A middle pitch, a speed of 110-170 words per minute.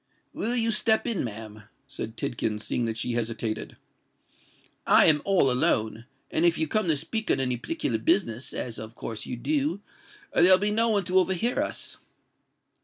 Yes: medium, 155 Hz; average, 160 wpm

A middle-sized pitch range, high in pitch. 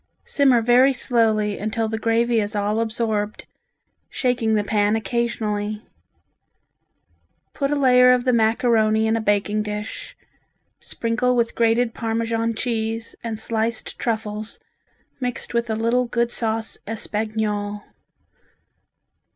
No: narrow, 1.6 semitones; high, 225 Hz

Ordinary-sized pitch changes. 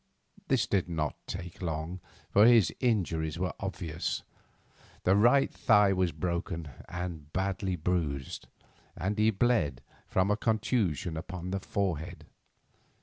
Yes: average, 3.7 semitones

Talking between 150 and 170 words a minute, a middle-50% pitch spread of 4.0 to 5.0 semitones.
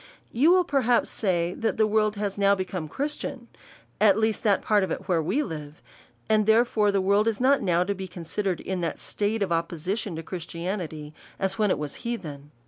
No: average, 195 wpm; average, 4.3 semitones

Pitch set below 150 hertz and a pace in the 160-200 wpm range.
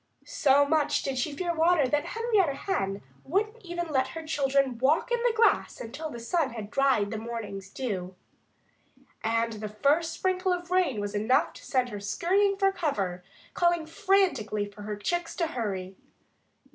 No: very high, 280 Hz; average, 170 wpm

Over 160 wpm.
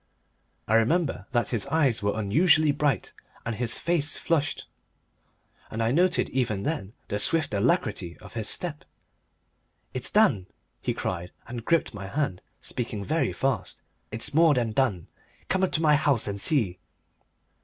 No: average, 155 wpm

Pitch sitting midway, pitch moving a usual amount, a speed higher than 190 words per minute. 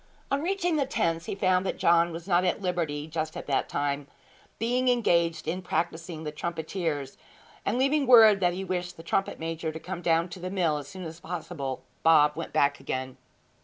Yes: medium, 170 Hz; average, 3.1 semitones; average, 200 wpm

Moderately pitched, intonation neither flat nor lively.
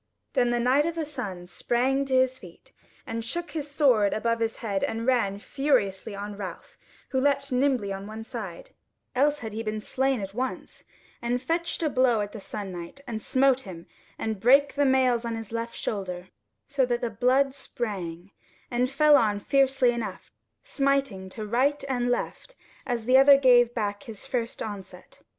No: high, 240 Hz; average, 4.4 semitones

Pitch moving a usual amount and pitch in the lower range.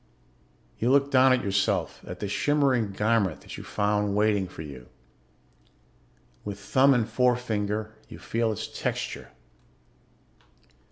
Yes: average, 3.6 semitones; low, 110 Hz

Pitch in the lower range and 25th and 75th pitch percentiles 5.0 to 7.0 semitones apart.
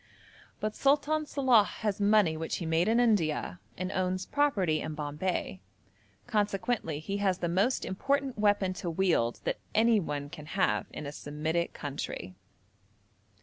No: medium, 185 Hz; wide, 5.5 semitones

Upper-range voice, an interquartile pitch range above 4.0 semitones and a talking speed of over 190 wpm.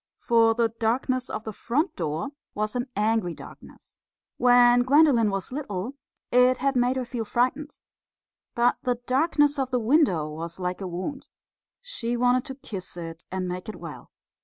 No: high, 240 Hz; average, 4.7 semitones; average, 165 wpm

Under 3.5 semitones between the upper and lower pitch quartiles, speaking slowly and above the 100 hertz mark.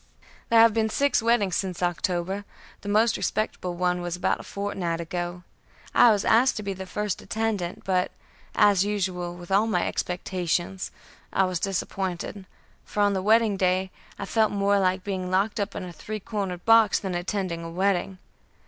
No: narrow, 2.6 semitones; average, 175 wpm; high, 190 Hz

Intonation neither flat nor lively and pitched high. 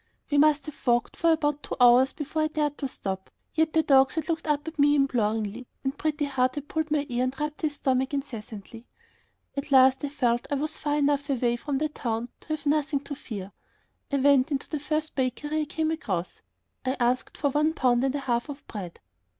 Yes: average, 3.1 semitones; very high, 280 Hz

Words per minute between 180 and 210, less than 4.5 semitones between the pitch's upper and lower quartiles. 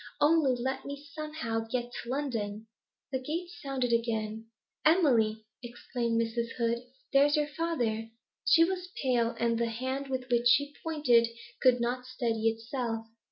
No: average, 145 wpm; average, 3.5 semitones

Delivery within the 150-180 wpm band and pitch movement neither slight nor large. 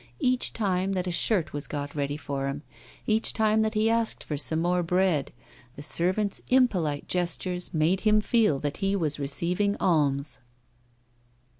No: average, 160 wpm; wide, 5.9 semitones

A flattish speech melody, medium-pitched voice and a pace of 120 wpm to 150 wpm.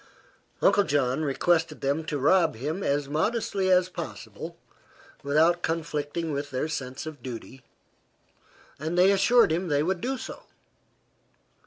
No: average, 4.1 semitones; medium, 155 Hz; slow, 135 wpm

